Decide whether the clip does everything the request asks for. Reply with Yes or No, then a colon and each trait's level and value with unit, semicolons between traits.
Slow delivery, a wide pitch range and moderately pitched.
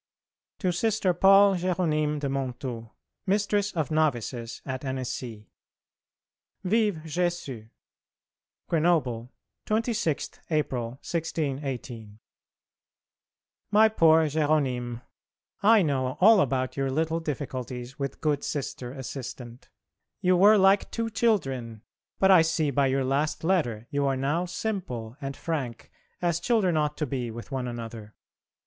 Yes: slow, 120 wpm; wide, 5.7 semitones; medium, 150 Hz